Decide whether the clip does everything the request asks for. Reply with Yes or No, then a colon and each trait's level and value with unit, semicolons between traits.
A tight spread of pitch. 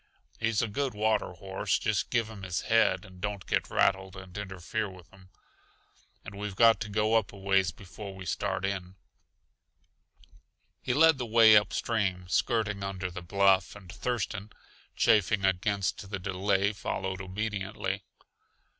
Yes: narrow, 2.3 semitones